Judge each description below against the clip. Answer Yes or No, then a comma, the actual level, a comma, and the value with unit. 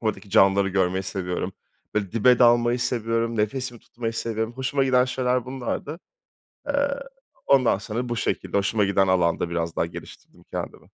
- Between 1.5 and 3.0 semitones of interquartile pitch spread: No, average, 4.2 semitones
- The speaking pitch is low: Yes, low, 115 Hz